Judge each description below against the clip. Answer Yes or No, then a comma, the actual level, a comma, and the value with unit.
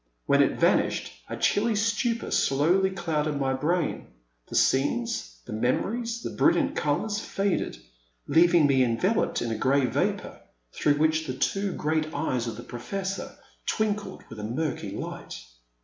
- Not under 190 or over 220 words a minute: No, average, 155 wpm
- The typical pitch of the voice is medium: Yes, medium, 160 Hz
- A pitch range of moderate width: No, wide, 7.3 semitones